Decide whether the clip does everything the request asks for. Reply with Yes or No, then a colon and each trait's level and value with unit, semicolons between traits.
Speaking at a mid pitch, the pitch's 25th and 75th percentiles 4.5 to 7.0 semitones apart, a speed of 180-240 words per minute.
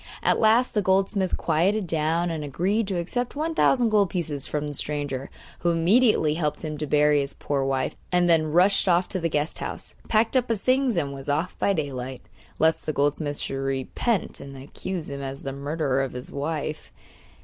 Yes: medium, 160 Hz; average, 5.2 semitones; average, 195 wpm